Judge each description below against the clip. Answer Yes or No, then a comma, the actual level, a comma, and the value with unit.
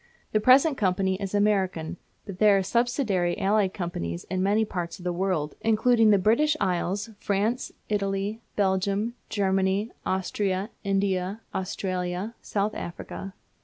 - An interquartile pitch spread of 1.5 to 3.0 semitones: Yes, narrow, 2.4 semitones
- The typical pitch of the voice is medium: No, high, 195 Hz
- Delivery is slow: Yes, slow, 130 wpm